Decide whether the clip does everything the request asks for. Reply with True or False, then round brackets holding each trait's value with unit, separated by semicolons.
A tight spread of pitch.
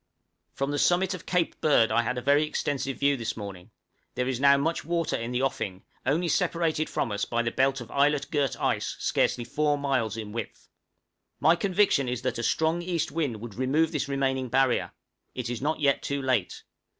False (4.2 semitones)